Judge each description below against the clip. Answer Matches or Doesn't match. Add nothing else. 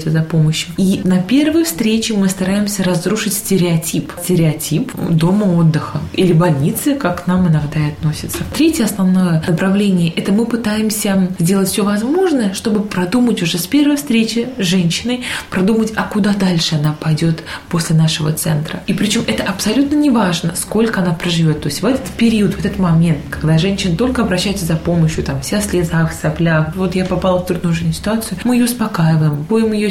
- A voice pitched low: Doesn't match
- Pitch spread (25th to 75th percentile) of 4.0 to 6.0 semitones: Matches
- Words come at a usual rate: Doesn't match